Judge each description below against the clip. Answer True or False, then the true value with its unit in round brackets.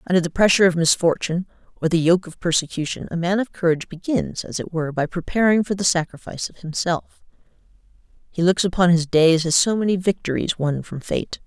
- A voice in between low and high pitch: True (175 Hz)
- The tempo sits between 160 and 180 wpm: False (195 wpm)